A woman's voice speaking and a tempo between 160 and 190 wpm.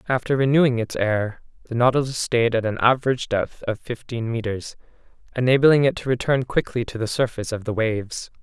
No: male; average, 180 wpm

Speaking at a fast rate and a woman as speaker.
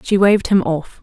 Yes: fast, 235 wpm; female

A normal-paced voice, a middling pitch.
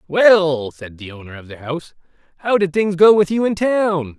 No: fast, 215 wpm; medium, 165 Hz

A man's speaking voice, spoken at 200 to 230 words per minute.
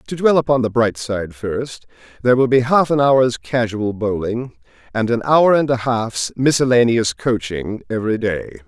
No: male; average, 175 wpm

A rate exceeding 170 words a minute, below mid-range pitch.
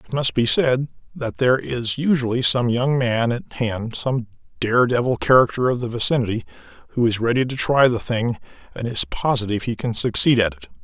Yes: average, 195 wpm; low, 115 Hz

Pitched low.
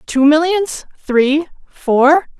No: very high, 300 Hz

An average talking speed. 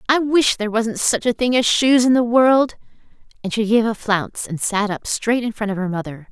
No: fast, 245 wpm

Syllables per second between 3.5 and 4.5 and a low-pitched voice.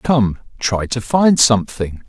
Yes: 3.8 syllables/s; low, 120 Hz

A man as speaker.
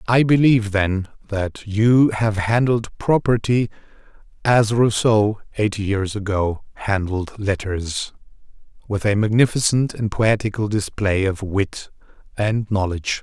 Yes: male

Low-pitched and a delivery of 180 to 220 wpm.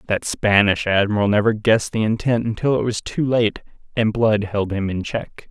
Yes: low, 110 Hz; average, 195 wpm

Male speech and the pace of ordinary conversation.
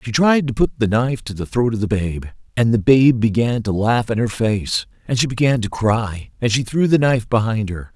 No: male; fast, 250 wpm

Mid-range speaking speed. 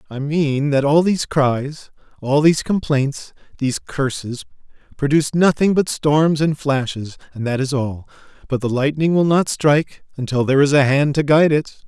Yes: average, 175 wpm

